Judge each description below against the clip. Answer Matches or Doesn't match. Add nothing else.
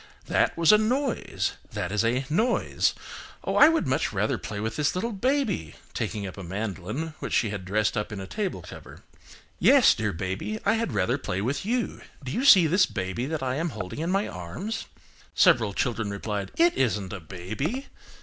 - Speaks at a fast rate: Doesn't match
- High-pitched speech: Doesn't match